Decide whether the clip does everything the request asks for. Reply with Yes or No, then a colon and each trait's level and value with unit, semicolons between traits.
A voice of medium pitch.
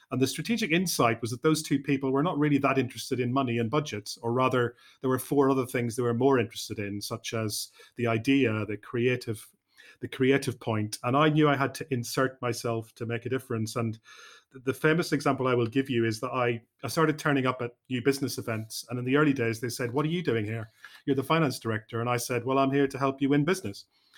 No: low, 130 Hz